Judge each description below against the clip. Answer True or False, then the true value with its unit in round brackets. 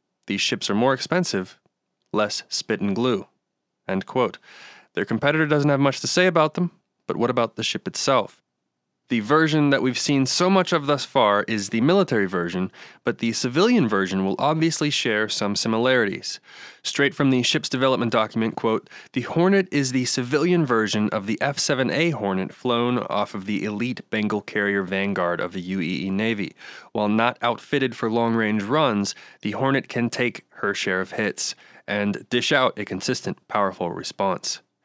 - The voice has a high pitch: False (120 Hz)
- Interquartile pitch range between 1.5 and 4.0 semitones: False (5.6 semitones)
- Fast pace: False (170 wpm)